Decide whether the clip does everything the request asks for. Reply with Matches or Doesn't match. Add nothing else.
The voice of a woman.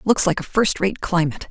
Matches